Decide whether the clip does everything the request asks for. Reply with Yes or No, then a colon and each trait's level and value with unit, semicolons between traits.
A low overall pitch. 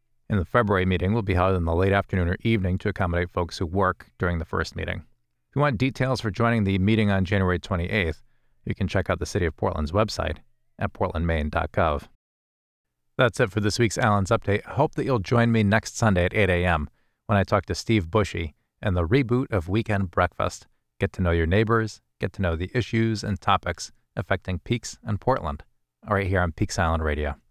Yes: very low, 95 Hz